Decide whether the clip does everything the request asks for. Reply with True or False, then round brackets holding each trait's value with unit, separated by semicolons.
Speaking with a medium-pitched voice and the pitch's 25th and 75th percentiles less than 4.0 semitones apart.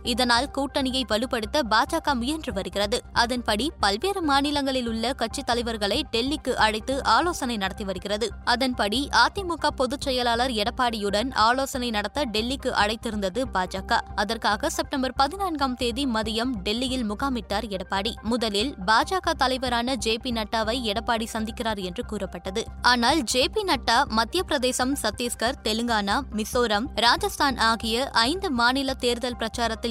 False (240 Hz; 3.6 semitones)